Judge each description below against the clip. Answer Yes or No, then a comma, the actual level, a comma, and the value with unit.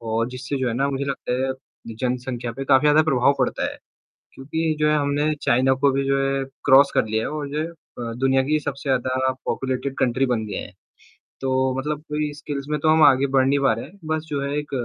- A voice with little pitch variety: Yes, narrow, 2.2 semitones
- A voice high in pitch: No, low, 135 Hz